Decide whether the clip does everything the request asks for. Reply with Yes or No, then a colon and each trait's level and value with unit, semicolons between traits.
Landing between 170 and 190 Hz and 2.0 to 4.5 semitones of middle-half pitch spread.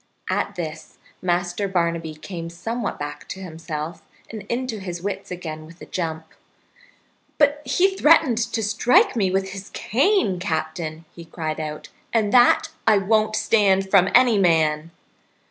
No: medium, 185 Hz; average, 5.1 semitones